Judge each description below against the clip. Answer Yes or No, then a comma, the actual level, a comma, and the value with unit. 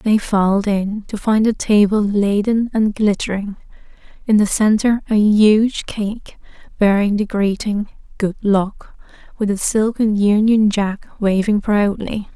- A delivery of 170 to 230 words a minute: No, slow, 135 wpm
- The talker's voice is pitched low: No, high, 210 Hz